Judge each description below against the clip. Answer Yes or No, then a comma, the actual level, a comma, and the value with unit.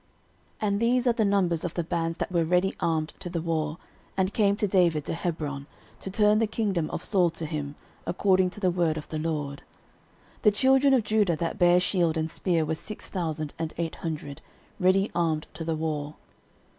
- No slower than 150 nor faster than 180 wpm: No, fast, 205 wpm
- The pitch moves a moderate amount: Yes, average, 3.8 semitones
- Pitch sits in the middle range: Yes, medium, 170 Hz